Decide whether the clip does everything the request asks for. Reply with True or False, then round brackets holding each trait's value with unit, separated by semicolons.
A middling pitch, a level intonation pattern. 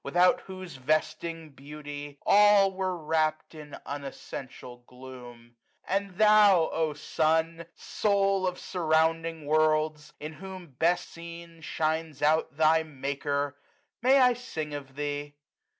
False (160 Hz; 3.4 semitones)